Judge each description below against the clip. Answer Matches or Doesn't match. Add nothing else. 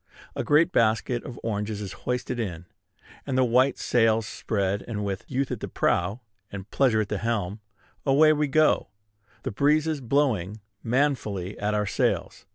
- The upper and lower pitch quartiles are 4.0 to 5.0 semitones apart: Matches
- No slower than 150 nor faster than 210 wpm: Matches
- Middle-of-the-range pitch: Doesn't match